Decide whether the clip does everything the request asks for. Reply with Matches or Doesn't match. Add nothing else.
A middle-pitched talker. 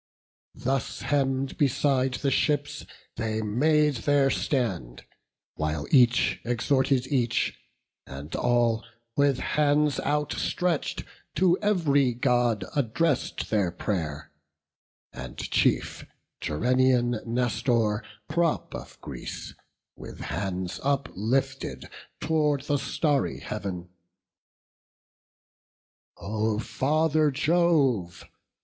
Doesn't match